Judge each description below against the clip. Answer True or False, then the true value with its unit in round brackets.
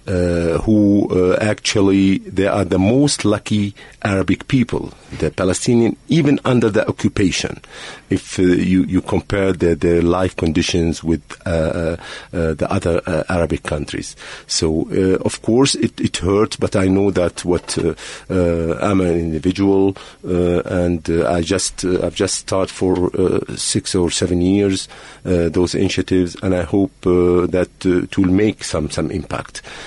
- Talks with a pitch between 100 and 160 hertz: False (90 Hz)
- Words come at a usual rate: True (165 wpm)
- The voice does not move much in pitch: True (2.0 semitones)